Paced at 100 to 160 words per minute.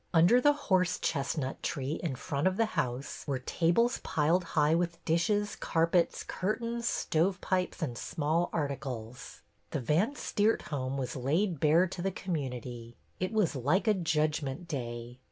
Yes: average, 150 wpm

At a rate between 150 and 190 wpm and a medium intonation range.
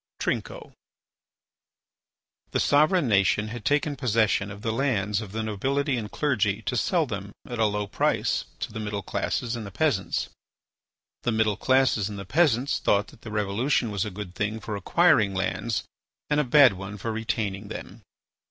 Yes: average, 170 wpm; average, 3.8 semitones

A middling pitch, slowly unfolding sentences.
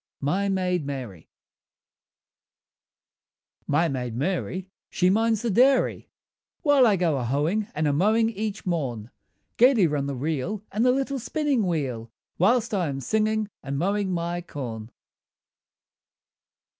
Yes: medium, 180 Hz; slow, 130 wpm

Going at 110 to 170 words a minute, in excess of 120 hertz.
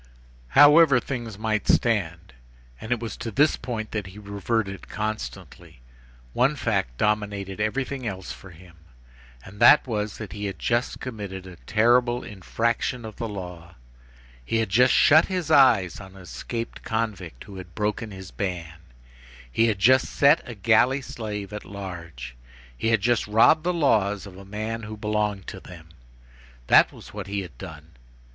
No: average, 160 wpm; low, 105 Hz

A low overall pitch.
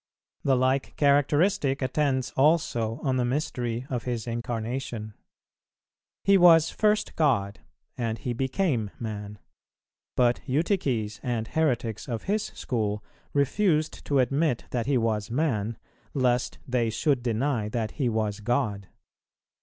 Yes: low, 125 Hz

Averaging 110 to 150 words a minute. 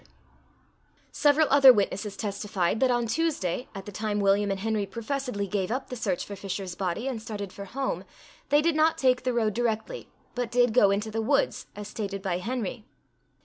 No: average, 190 wpm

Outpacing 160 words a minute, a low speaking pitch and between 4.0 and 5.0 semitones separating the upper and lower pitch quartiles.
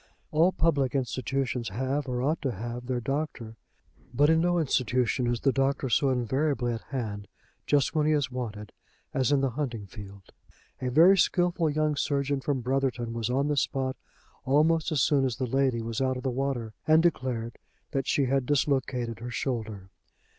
No: average, 180 wpm; low, 130 Hz; average, 3.1 semitones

